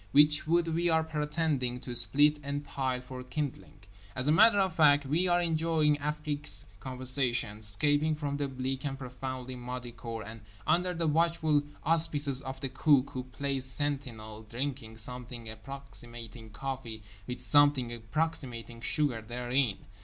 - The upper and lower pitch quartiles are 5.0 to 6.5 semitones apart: No, average, 3.5 semitones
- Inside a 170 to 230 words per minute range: No, average, 145 wpm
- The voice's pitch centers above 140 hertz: No, low, 135 Hz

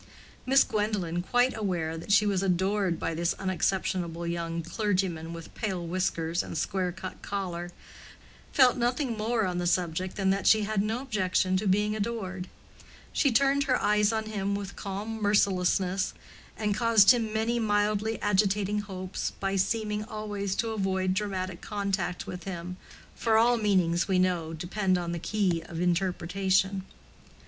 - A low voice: No, high, 195 Hz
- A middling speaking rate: Yes, average, 155 wpm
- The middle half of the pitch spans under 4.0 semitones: Yes, average, 2.8 semitones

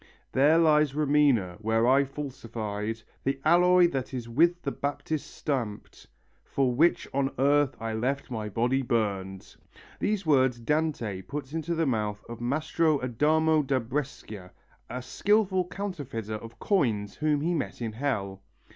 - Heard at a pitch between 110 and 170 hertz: Yes, low, 135 Hz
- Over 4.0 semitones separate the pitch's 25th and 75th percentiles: Yes, average, 5.2 semitones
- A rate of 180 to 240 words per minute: No, average, 145 wpm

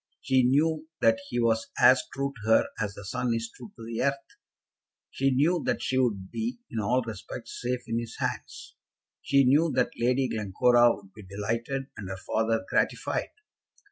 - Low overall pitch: Yes, low, 120 Hz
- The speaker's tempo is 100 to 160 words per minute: No, average, 180 wpm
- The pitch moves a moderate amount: Yes, average, 3.1 semitones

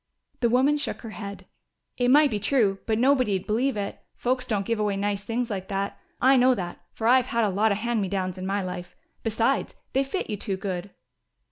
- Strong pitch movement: No, average, 4.0 semitones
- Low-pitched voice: No, high, 215 Hz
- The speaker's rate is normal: No, fast, 220 wpm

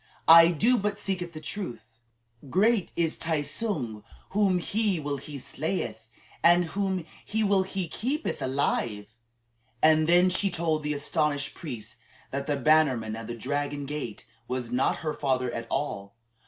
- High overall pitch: No, medium, 155 Hz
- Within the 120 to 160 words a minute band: Yes, average, 155 wpm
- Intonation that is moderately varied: No, wide, 6.1 semitones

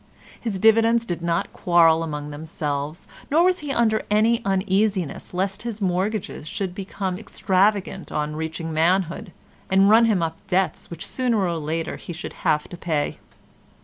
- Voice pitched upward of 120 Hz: Yes, medium, 185 Hz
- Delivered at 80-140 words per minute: No, average, 155 wpm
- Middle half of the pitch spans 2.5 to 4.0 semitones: No, average, 4.7 semitones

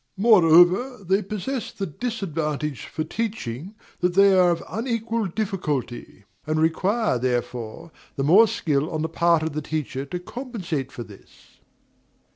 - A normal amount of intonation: No, wide, 5.7 semitones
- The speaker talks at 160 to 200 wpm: No, average, 140 wpm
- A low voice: No, medium, 175 Hz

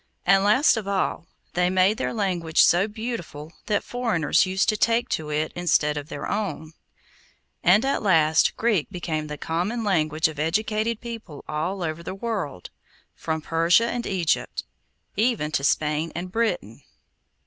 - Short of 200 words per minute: Yes, average, 160 wpm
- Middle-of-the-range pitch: Yes, medium, 180 Hz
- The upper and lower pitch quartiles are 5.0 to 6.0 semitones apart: Yes, wide, 5.4 semitones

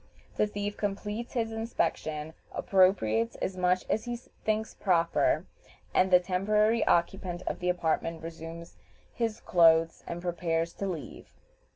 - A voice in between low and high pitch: Yes, medium, 180 Hz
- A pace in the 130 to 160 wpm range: Yes, slow, 135 wpm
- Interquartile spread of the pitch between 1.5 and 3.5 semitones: No, average, 4.0 semitones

